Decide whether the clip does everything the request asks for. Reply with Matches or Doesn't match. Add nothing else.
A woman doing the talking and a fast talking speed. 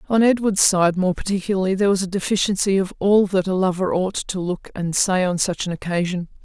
Matches